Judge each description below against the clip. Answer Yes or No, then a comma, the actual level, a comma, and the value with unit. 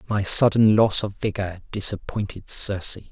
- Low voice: Yes, low, 100 Hz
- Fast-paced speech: No, slow, 135 wpm